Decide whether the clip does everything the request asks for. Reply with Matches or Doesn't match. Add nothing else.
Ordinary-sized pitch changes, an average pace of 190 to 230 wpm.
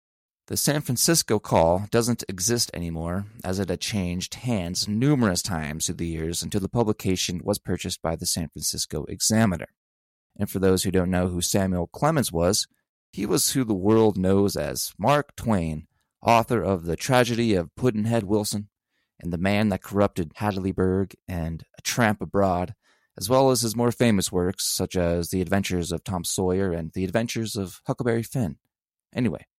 Doesn't match